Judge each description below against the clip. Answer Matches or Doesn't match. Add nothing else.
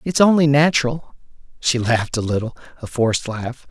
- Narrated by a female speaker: Doesn't match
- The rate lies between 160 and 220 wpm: Doesn't match